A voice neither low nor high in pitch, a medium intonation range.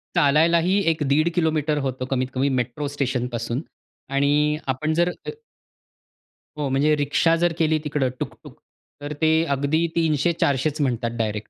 Yes: medium, 145 Hz; average, 3.1 semitones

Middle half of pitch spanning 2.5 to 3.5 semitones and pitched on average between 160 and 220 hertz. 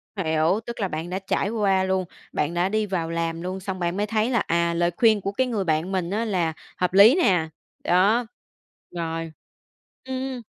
No: average, 4.0 semitones; high, 190 Hz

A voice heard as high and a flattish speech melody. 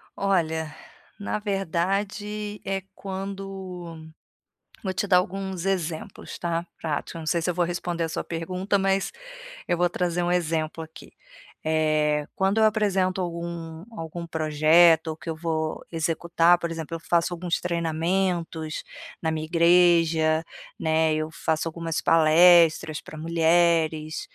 No: medium, 170 Hz; narrow, 2.3 semitones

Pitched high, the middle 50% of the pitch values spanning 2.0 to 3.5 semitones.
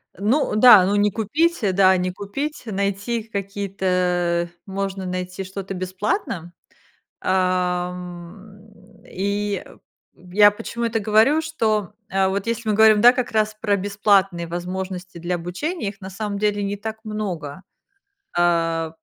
Yes: high, 195 Hz; average, 2.8 semitones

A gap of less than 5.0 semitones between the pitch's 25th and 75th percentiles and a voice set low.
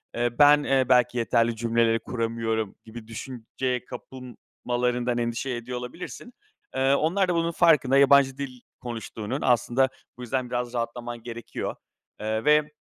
Yes: narrow, 2.4 semitones; low, 125 Hz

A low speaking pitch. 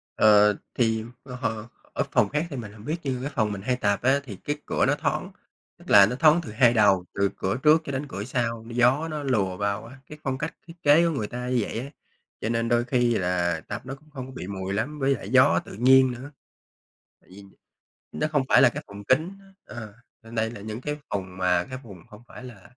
Yes: low, 120 Hz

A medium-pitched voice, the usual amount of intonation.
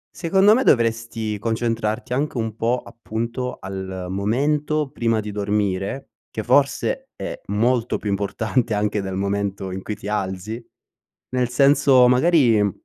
No: low, 115 Hz; average, 3.8 semitones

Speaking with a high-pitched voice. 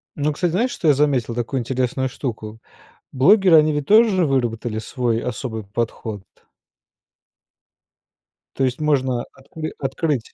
No: low, 130 Hz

